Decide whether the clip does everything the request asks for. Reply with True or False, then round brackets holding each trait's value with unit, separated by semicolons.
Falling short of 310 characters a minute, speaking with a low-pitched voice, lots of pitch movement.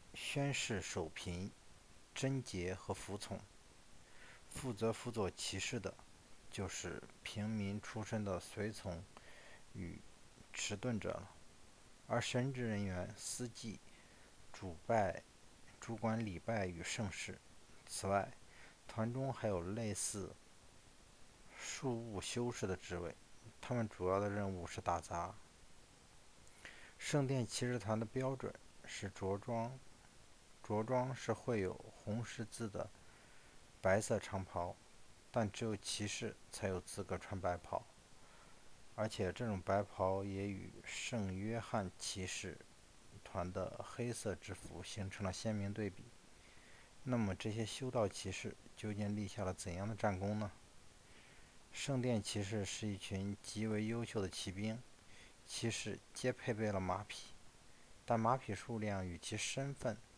False (180 characters per minute; 105 Hz; 3.5 semitones)